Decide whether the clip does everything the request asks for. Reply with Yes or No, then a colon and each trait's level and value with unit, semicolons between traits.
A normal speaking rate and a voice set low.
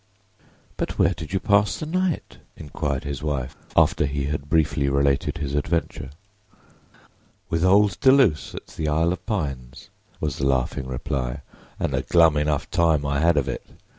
Yes: average, 165 wpm; very low, 75 Hz